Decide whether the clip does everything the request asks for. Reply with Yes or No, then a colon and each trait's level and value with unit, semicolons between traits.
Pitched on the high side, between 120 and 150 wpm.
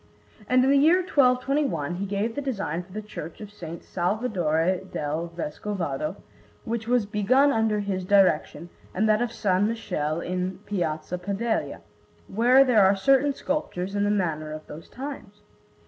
No: high, 200 Hz; average, 160 wpm